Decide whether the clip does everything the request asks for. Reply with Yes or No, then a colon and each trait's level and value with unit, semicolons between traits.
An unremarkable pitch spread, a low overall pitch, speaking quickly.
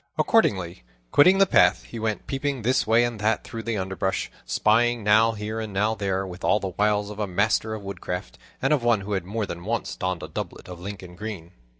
Yes: average, 3.0 semitones; low, 105 Hz; fast, 220 wpm